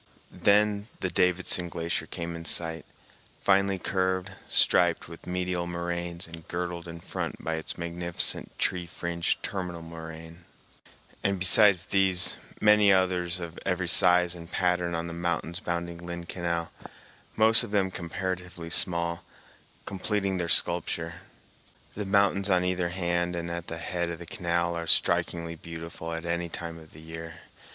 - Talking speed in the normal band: Yes, average, 150 wpm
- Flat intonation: Yes, narrow, 1.6 semitones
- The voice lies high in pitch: No, very low, 85 Hz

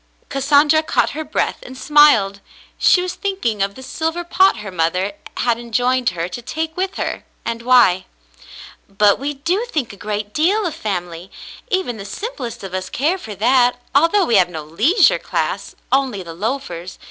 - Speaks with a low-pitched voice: No, high, 245 Hz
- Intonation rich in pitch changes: Yes, wide, 7.8 semitones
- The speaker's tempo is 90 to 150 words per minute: No, average, 180 wpm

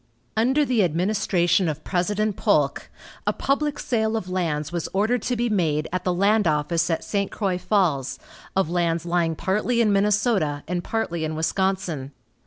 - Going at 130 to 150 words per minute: No, average, 165 wpm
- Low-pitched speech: No, medium, 185 Hz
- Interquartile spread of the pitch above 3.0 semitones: Yes, average, 4.3 semitones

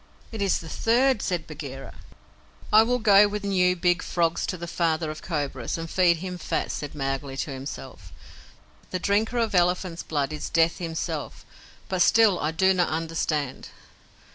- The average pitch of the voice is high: No, medium, 170 Hz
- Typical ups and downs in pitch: Yes, average, 3.8 semitones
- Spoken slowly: No, average, 165 wpm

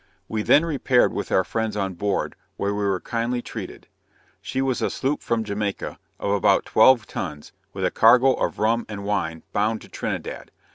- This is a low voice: Yes, low, 110 Hz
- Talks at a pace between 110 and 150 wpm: No, average, 185 wpm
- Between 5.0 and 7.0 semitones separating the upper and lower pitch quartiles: No, average, 3.3 semitones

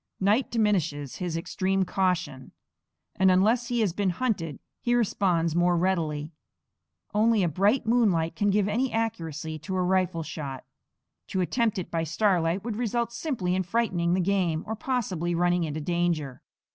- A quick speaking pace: No, average, 160 wpm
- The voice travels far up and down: No, average, 4.5 semitones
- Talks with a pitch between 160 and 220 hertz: Yes, medium, 185 Hz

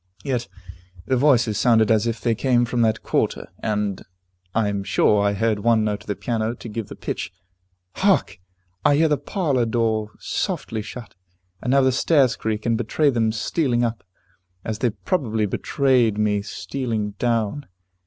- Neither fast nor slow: Yes, average, 175 wpm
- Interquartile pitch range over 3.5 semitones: No, average, 3.0 semitones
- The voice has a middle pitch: No, low, 115 Hz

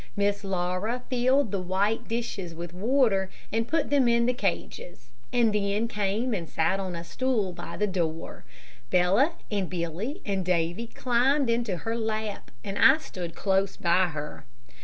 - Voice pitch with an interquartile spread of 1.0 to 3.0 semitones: No, average, 4.5 semitones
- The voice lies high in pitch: Yes, high, 200 Hz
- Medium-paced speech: Yes, average, 165 wpm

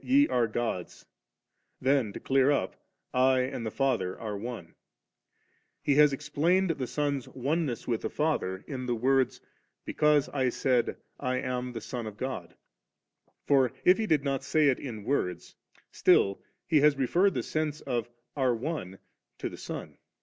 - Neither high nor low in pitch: No, low, 130 Hz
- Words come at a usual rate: Yes, average, 170 wpm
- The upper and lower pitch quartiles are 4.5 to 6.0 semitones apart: No, average, 3.6 semitones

